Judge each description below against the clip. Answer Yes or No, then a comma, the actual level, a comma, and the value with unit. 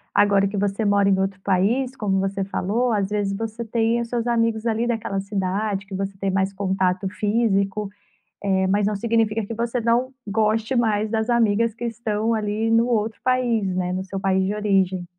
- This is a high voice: Yes, high, 210 Hz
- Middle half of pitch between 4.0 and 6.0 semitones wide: No, average, 2.7 semitones